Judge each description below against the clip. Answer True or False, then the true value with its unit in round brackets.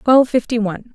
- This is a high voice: True (235 Hz)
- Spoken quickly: False (190 wpm)